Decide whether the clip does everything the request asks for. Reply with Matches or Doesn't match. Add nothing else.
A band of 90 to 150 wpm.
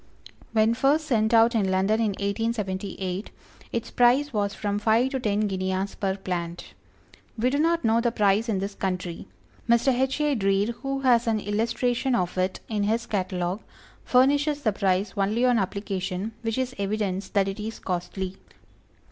Doesn't match